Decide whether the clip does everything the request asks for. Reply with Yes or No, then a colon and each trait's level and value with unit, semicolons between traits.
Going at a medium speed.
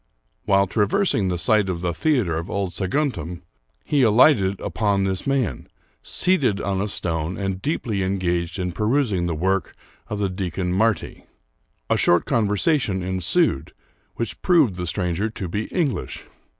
Yes: average, 150 wpm